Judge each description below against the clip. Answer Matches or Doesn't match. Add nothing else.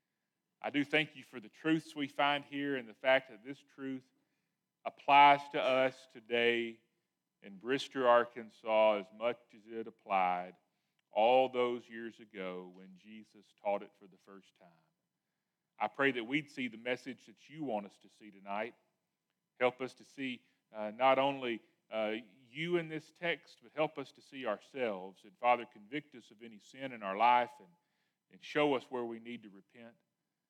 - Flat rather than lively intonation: Doesn't match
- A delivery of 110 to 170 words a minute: Doesn't match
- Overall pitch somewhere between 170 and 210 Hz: Doesn't match